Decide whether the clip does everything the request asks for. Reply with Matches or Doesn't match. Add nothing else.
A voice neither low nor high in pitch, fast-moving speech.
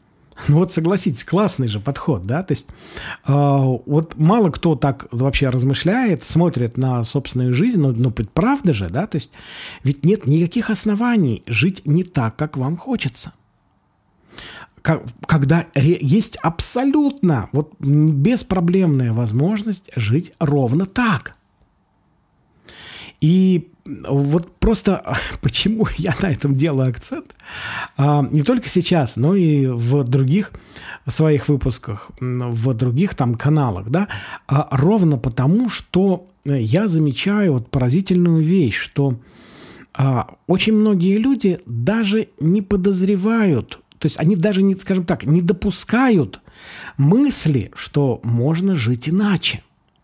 Doesn't match